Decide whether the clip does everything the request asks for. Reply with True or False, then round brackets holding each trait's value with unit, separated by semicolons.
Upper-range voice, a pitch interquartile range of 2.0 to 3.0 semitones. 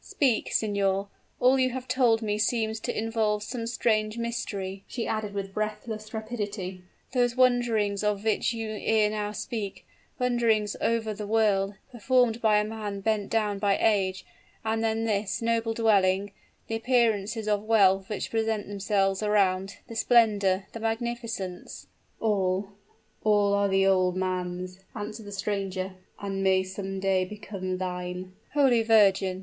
True (210 Hz; 2.5 semitones)